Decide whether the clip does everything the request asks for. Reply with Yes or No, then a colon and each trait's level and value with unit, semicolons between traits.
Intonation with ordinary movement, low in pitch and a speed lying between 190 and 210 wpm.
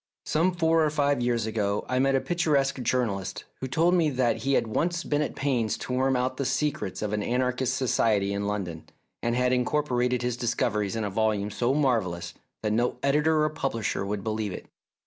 Yes: average, 4.6 semitones; low, 125 Hz; fast, 205 wpm